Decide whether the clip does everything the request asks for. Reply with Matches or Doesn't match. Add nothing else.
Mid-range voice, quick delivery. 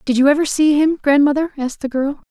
Doesn't match